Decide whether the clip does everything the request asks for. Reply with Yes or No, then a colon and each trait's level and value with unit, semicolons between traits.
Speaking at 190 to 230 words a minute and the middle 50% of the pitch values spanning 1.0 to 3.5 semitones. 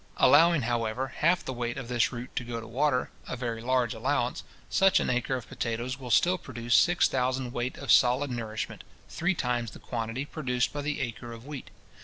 Yes: average, 200 wpm; narrow, 2.5 semitones